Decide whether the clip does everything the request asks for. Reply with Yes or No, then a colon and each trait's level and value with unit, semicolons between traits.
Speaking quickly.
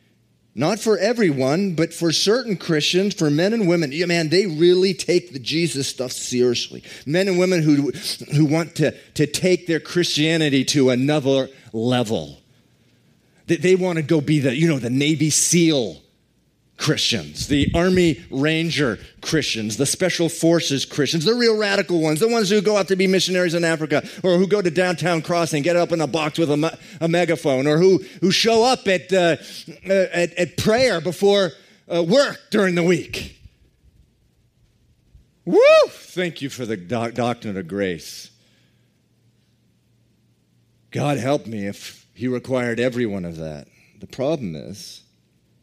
No: average, 160 wpm